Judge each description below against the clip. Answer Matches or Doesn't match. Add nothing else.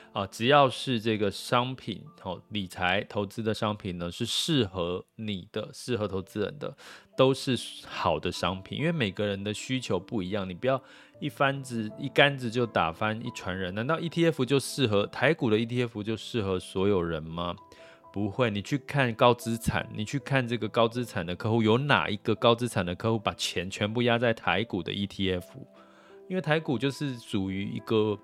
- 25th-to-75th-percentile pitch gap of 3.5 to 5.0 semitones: Matches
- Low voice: Matches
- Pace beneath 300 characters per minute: Matches